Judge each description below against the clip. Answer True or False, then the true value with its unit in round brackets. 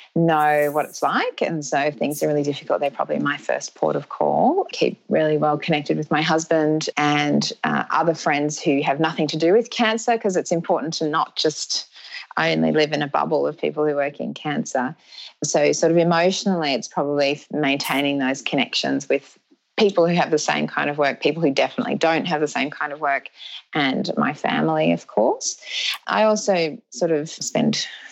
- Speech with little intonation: True (2.3 semitones)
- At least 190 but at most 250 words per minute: True (195 wpm)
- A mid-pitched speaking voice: True (155 Hz)